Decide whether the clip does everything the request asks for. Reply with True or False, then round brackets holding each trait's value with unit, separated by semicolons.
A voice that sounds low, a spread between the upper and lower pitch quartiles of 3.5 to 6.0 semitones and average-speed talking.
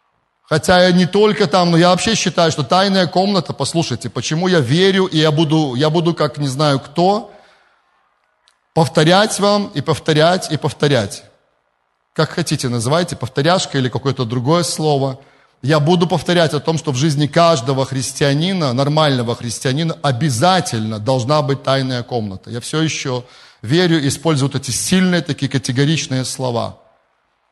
False (150 Hz; 4.6 semitones; 145 wpm)